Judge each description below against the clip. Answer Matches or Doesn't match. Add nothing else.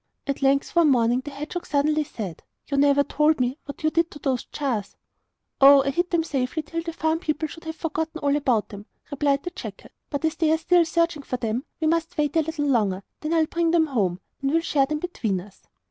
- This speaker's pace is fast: Matches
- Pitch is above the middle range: Matches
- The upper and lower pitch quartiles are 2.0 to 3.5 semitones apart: Matches